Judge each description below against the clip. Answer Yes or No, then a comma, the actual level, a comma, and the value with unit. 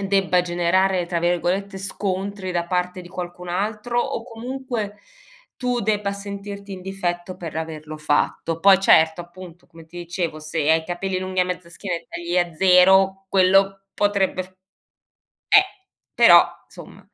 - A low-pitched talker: No, medium, 185 Hz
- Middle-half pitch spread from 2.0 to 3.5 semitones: Yes, narrow, 2.3 semitones